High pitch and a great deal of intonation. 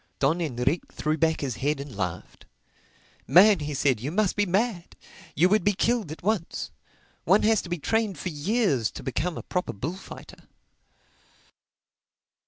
No: medium, 170 Hz; wide, 6.0 semitones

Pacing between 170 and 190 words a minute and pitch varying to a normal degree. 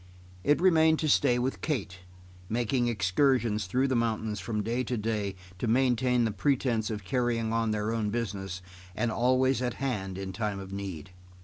Yes: average, 175 wpm; average, 3.5 semitones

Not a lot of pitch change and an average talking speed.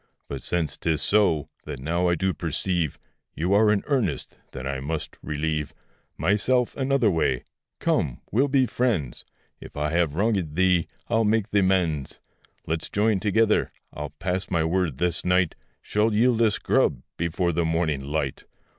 No: average, 5.2 semitones; average, 160 wpm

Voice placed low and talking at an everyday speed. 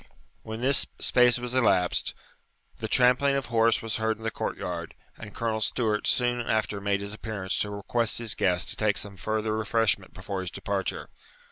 Yes: low, 110 Hz; average, 180 wpm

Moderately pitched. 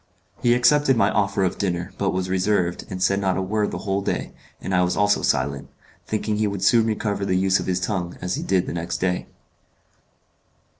No: very low, 95 Hz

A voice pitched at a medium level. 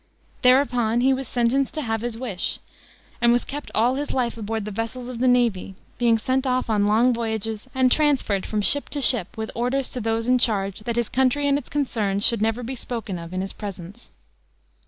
No: high, 235 Hz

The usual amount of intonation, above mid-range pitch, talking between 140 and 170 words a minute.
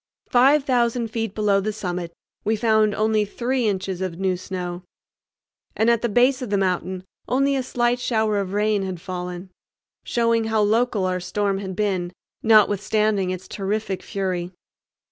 Yes: average, 3.4 semitones; high, 210 Hz; average, 160 wpm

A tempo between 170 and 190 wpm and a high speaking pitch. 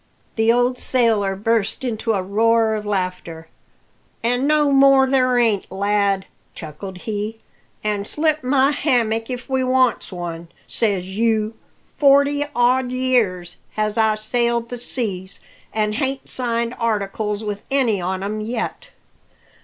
No: slow, 135 wpm; high, 225 Hz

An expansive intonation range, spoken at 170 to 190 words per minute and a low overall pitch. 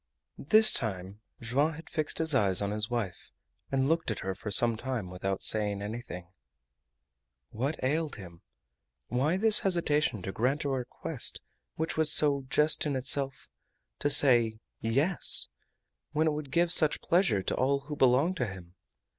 No: wide, 6.1 semitones; average, 160 wpm; low, 130 Hz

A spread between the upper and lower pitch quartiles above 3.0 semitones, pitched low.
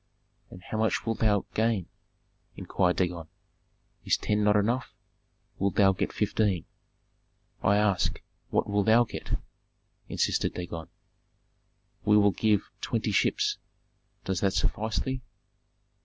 No: average, 2.7 semitones; low, 105 Hz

